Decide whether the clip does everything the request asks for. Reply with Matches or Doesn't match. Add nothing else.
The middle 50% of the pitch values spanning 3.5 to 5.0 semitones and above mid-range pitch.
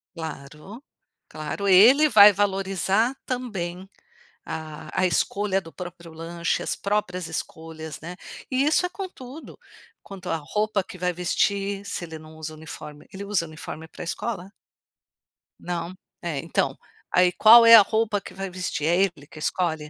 Doesn't match